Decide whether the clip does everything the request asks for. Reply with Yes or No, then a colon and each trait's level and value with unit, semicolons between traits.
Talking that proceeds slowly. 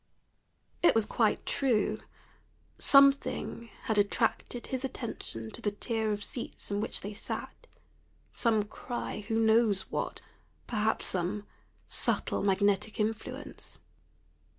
Yes: slow, 115 wpm